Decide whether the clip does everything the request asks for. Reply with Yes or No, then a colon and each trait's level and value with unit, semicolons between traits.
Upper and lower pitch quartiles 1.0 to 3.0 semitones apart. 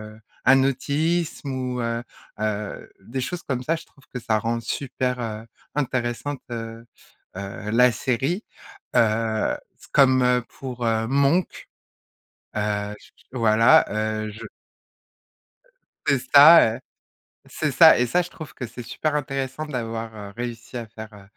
No: average, 3.5 semitones